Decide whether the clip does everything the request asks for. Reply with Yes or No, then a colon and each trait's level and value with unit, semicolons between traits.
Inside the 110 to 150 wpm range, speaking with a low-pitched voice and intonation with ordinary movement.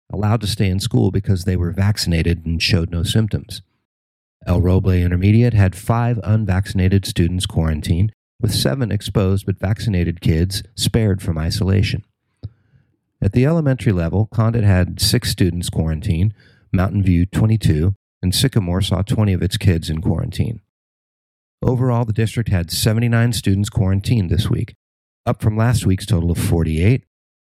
Yes: average, 145 wpm; low, 100 Hz; average, 4.1 semitones